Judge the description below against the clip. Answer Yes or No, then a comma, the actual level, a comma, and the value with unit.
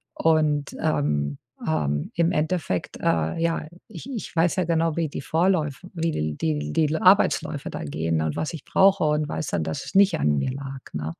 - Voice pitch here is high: No, medium, 150 Hz